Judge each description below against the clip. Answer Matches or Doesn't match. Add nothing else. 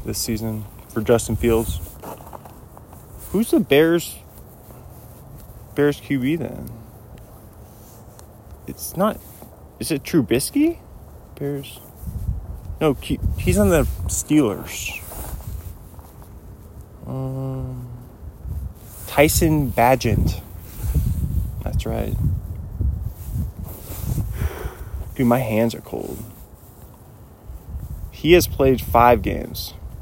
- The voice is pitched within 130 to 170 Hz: Doesn't match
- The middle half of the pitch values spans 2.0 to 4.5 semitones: Doesn't match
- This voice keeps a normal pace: Doesn't match